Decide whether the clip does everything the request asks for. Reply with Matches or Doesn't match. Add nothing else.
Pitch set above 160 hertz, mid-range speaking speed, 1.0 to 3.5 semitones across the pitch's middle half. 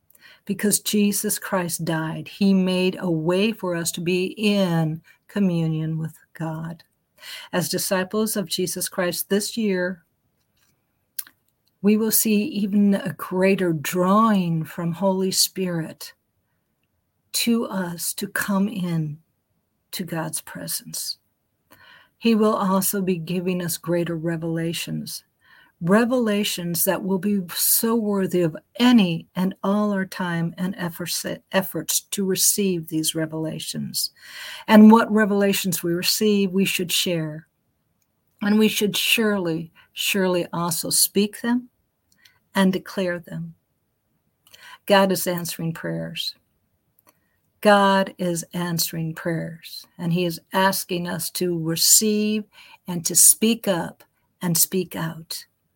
Doesn't match